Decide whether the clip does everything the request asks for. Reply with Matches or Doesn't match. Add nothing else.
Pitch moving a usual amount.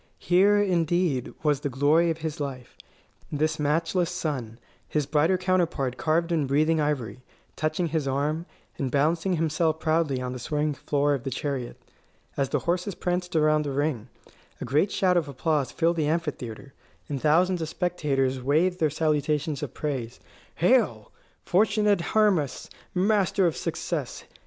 Matches